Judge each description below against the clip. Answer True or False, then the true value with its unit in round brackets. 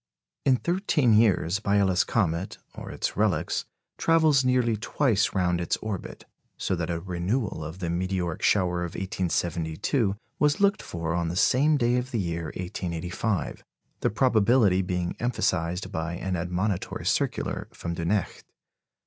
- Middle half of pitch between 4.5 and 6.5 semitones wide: True (5.1 semitones)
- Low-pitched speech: True (95 Hz)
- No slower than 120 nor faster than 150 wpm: True (140 wpm)